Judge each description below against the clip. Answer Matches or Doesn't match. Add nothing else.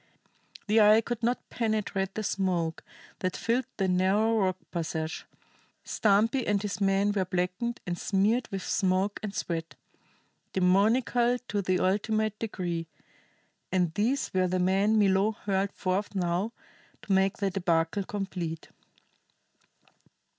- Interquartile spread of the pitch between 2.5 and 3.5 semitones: Matches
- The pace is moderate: Doesn't match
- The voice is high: Matches